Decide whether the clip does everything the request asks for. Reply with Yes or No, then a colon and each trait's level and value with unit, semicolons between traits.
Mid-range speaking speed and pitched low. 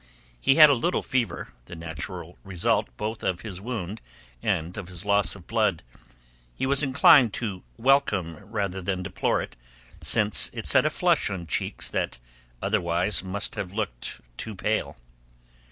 Yes: average, 155 wpm; low, 100 Hz